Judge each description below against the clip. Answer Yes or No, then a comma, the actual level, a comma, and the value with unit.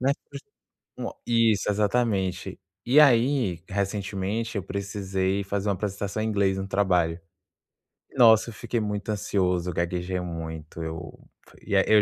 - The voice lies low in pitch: Yes, low, 100 Hz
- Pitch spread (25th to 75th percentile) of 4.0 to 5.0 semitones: No, average, 2.9 semitones